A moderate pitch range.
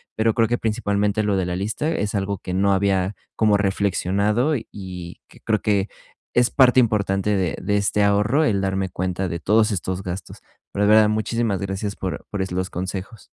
No: narrow, 2.2 semitones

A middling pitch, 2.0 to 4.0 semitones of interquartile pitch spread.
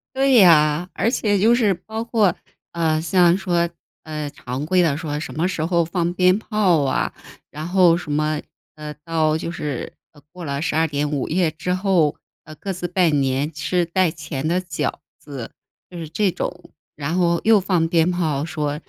Yes: medium, 170 Hz; average, 3.1 semitones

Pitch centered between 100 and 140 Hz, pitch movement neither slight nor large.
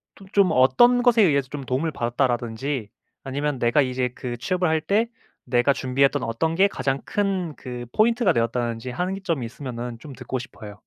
No: low, 135 Hz; wide, 6.4 semitones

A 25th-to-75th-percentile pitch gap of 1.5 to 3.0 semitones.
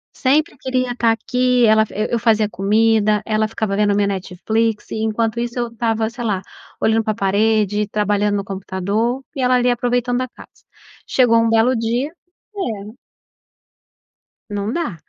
Yes: average, 2.7 semitones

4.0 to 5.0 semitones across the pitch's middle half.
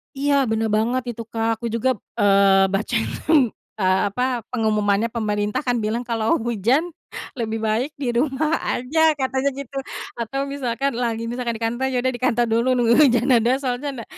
No: average, 2.9 semitones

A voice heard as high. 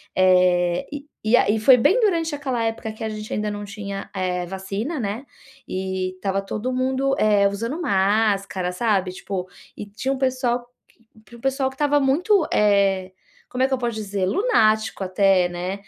Yes: high, 215 Hz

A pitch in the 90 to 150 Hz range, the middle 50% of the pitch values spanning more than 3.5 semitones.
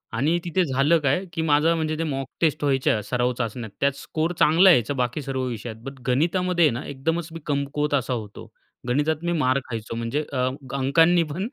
Yes: medium, 140 Hz; average, 4.3 semitones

